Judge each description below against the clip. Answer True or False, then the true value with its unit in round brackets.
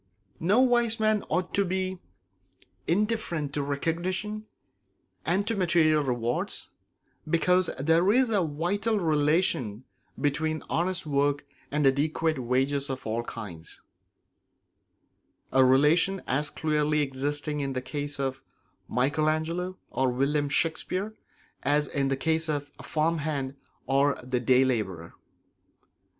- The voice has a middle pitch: True (150 Hz)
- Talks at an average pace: False (125 wpm)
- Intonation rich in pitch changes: False (4.5 semitones)